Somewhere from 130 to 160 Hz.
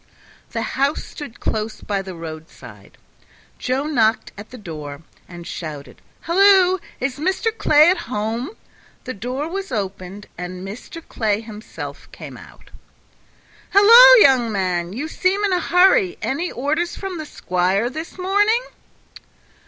No: very high, 250 Hz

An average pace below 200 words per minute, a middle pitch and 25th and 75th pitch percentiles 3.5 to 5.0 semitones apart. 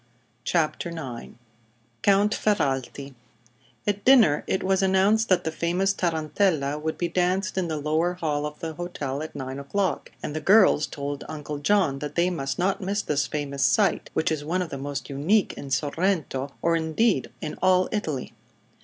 Yes: average, 170 wpm; medium, 160 Hz; average, 4.6 semitones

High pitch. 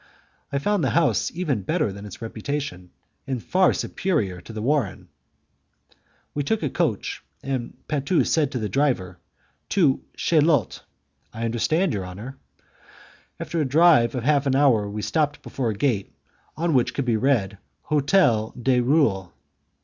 No: low, 130 Hz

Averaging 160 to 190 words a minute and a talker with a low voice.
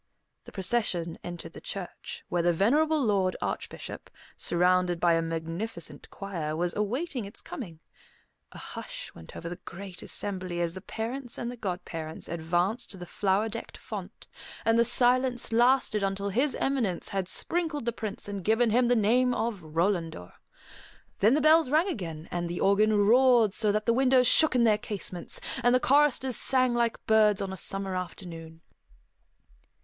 No: average, 165 wpm; high, 205 Hz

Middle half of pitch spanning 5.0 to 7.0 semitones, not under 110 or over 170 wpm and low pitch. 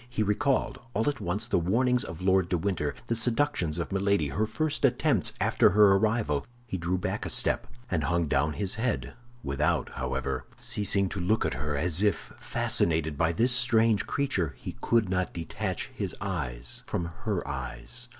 No: average, 5.3 semitones; average, 180 wpm; very low, 95 Hz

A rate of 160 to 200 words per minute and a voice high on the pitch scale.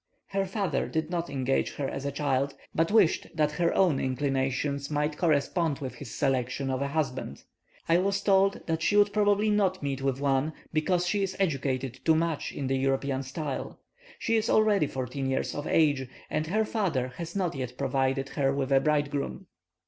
No: average, 185 wpm; medium, 145 Hz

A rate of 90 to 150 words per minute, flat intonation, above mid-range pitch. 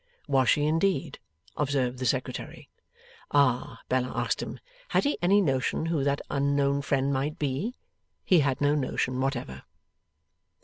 No: average, 140 wpm; narrow, 2.3 semitones; medium, 140 Hz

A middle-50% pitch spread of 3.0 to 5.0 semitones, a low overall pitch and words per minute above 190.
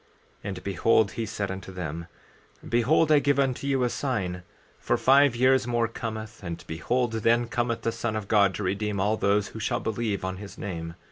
Yes: average, 3.7 semitones; low, 110 Hz; average, 200 wpm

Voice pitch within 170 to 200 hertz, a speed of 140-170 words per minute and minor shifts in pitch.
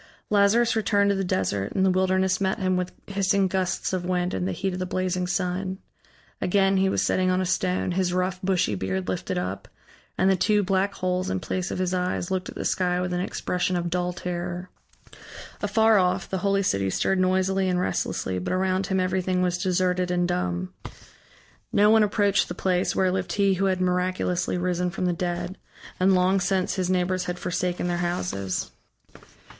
No: medium, 185 Hz; average, 195 wpm; narrow, 1.2 semitones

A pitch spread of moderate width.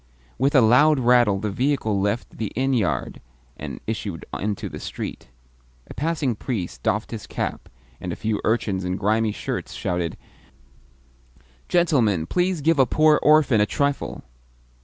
No: wide, 5.7 semitones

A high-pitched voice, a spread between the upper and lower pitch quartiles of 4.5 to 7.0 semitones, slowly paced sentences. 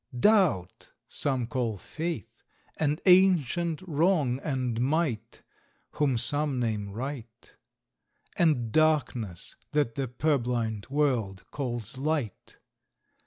No: low, 135 Hz; average, 4.9 semitones; slow, 95 wpm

